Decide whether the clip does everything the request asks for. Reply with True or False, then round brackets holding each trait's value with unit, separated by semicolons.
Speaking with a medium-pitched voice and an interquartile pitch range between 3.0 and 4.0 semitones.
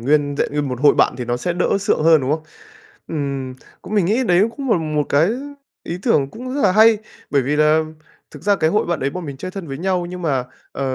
False (160 Hz; 5.1 semitones)